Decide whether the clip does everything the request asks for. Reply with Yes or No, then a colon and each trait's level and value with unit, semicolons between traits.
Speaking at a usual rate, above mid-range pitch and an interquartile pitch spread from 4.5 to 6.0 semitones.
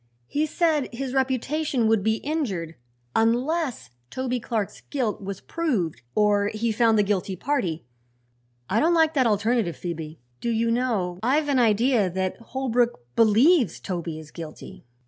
Yes: average, 145 wpm; high, 230 Hz; average, 5.2 semitones